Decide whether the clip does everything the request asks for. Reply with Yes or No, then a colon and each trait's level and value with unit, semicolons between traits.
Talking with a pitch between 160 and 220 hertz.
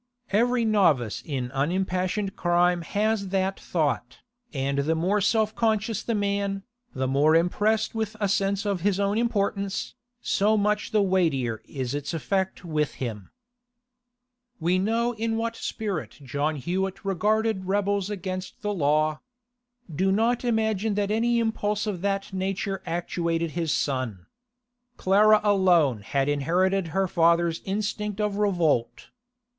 Yes: high, 190 Hz